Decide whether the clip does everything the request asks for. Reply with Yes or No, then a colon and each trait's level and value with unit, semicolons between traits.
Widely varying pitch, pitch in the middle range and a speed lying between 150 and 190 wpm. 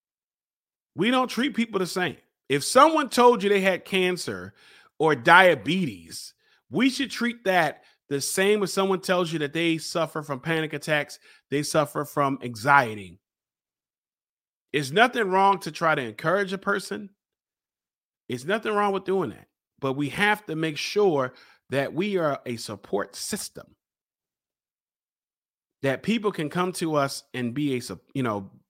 Yes: wide, 6.2 semitones; medium, 165 Hz; average, 155 wpm